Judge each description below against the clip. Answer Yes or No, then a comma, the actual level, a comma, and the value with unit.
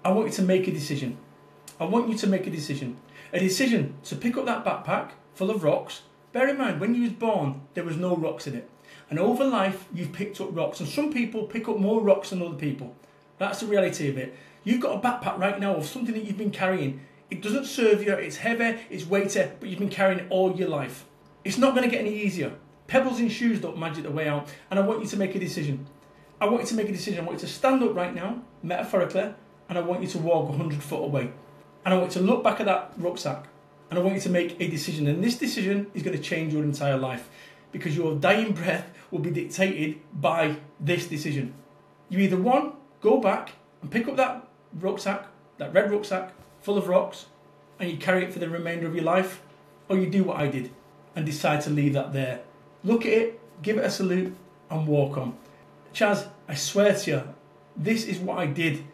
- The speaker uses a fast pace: Yes, fast, 235 wpm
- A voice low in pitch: No, medium, 185 Hz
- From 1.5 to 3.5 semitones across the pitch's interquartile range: No, average, 4.8 semitones